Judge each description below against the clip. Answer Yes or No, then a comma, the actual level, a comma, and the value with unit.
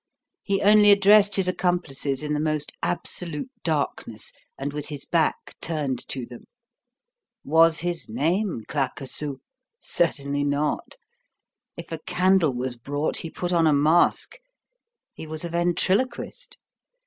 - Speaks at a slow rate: Yes, slow, 130 wpm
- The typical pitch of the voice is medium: Yes, medium, 160 Hz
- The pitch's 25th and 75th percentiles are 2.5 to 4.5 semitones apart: Yes, average, 3.9 semitones